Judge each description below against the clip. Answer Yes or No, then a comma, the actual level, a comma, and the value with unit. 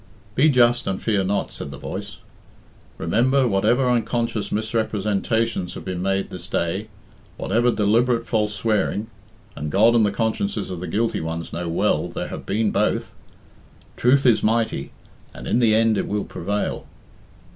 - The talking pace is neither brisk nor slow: Yes, average, 155 wpm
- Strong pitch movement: No, average, 3.3 semitones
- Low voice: Yes, low, 110 Hz